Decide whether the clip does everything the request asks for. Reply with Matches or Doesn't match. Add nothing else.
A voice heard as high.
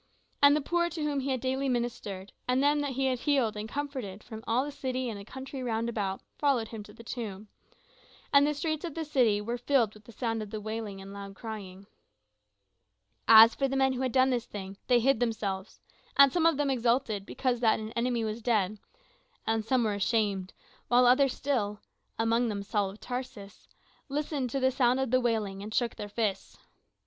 Matches